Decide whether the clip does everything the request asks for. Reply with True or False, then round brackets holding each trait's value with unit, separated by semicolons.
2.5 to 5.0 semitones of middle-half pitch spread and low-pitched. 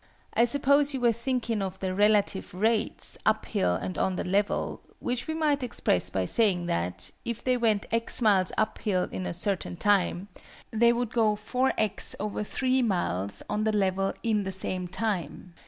False (4.1 semitones; 210 Hz)